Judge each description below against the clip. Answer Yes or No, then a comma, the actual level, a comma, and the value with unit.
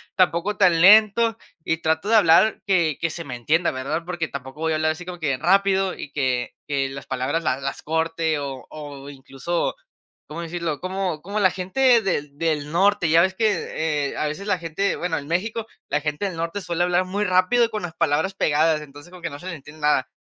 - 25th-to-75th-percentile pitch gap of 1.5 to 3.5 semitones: No, average, 4.0 semitones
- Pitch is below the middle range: No, medium, 165 Hz